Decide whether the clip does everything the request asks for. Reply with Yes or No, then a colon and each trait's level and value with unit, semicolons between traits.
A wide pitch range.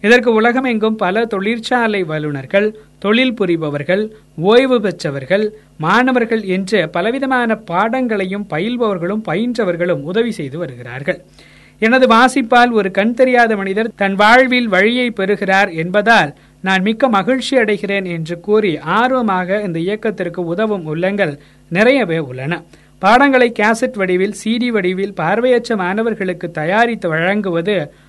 No: average, 4.3 semitones